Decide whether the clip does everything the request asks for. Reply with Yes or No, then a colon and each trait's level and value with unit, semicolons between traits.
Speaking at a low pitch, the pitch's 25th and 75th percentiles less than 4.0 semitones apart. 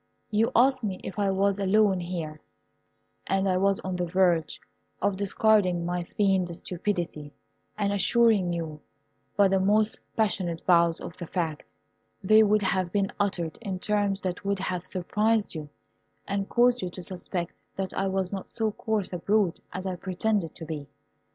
No: high, 190 Hz; average, 2.7 semitones